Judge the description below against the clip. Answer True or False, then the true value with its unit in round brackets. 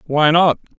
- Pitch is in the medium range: True (155 Hz)